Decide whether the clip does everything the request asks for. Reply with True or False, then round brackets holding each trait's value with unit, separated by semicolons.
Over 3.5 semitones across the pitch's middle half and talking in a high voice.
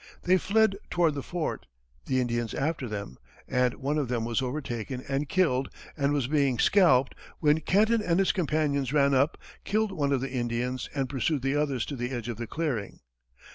False (3.9 semitones; 140 Hz)